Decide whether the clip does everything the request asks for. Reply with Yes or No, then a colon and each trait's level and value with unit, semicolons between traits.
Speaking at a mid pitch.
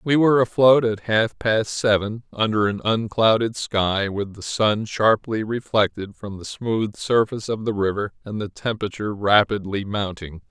No: low, 110 Hz